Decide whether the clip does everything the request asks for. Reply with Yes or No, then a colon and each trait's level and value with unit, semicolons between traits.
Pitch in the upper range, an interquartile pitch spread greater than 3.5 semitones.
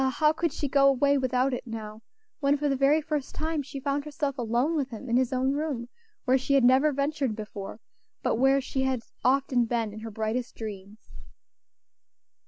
No: very high, 265 Hz; average, 3.1 semitones